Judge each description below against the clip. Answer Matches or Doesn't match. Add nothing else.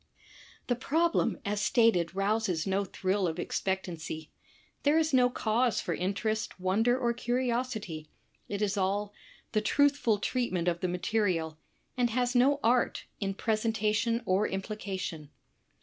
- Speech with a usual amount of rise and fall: Matches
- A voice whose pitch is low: Doesn't match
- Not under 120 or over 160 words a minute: Matches